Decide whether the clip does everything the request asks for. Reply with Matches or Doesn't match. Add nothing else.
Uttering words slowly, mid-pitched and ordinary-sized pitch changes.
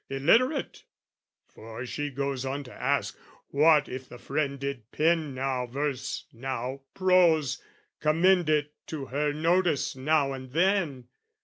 Matches